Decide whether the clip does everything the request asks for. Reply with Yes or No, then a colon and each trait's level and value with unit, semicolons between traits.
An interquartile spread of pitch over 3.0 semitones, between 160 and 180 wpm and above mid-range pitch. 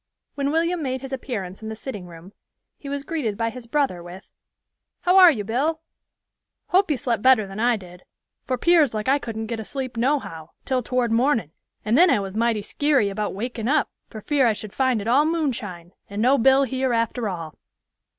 No: average, 4.7 semitones; average, 200 wpm; high, 240 Hz